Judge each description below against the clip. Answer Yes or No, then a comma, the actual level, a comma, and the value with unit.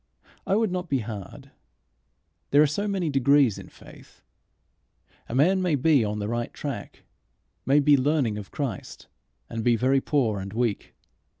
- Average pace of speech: Yes, average, 165 wpm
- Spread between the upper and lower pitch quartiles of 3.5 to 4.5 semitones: No, average, 4.9 semitones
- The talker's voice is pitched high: No, low, 135 Hz